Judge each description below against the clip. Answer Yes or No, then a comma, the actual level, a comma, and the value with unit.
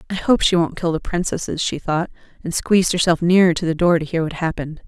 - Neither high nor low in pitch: Yes, medium, 170 Hz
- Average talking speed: No, fast, 245 wpm